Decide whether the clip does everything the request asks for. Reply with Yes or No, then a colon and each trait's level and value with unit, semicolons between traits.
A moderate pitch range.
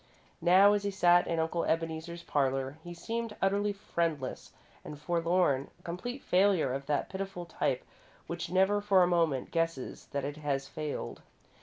Yes: average, 4.3 semitones